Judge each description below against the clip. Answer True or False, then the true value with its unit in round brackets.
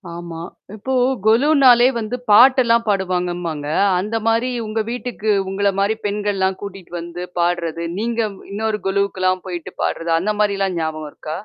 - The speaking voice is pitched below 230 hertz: True (200 Hz)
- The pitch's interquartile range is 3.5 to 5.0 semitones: True (4.1 semitones)